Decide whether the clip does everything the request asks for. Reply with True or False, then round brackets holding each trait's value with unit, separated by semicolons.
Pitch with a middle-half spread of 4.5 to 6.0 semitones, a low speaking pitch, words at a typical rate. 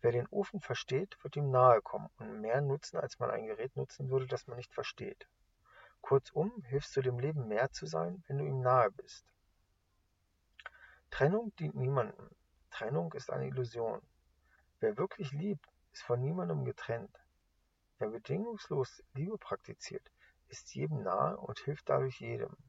True (5.5 semitones; 130 Hz; 155 wpm)